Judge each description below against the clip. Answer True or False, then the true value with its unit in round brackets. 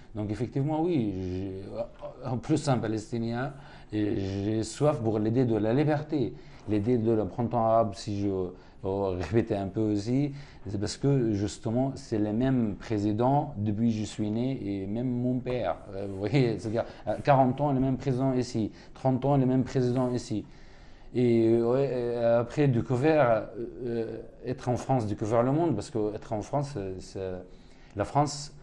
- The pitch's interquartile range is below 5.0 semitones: True (3.8 semitones)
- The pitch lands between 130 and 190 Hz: False (115 Hz)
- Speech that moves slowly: False (160 wpm)